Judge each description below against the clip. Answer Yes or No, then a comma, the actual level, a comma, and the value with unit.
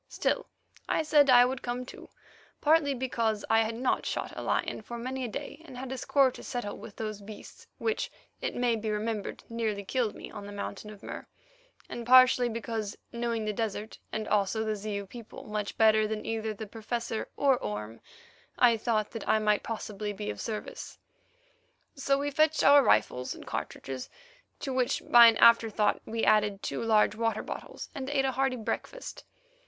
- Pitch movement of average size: Yes, average, 3.1 semitones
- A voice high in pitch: Yes, high, 225 Hz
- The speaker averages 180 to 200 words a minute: Yes, average, 185 wpm